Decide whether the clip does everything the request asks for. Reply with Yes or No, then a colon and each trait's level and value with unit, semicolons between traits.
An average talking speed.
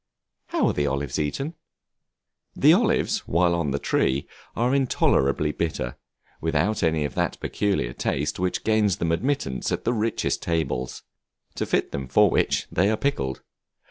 Yes: average, 155 wpm